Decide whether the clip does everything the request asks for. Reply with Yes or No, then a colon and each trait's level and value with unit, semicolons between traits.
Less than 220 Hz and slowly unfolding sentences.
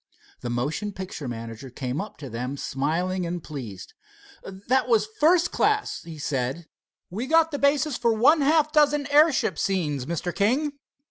No: high, 190 Hz; average, 155 wpm